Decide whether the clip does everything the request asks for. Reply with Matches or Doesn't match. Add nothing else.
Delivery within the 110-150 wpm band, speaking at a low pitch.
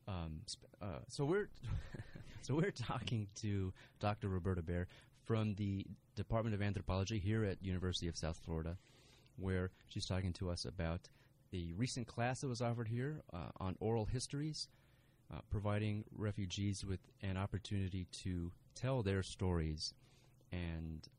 Matches